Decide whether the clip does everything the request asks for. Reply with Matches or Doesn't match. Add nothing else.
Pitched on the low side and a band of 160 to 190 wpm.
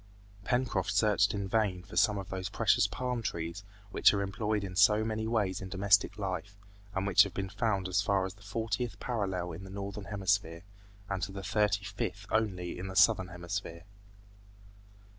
Matches